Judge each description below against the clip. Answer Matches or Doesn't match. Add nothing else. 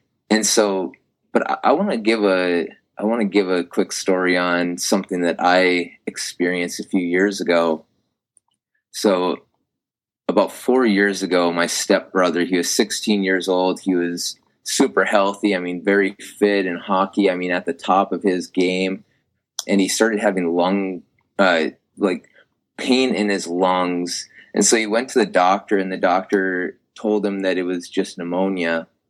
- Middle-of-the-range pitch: Doesn't match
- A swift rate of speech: Doesn't match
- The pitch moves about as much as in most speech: Doesn't match